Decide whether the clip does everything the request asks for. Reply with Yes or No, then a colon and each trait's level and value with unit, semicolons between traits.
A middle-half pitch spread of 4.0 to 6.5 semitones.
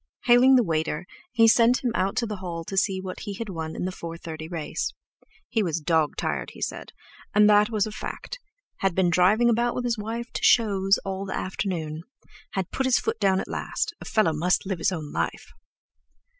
Yes: average, 4.8 semitones